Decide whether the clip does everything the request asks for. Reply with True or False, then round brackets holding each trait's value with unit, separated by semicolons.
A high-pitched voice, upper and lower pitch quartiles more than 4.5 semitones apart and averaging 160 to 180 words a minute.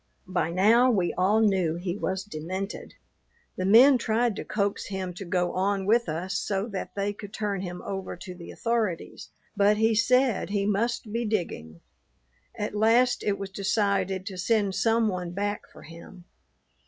False (200 Hz; 2.9 semitones; 170 wpm)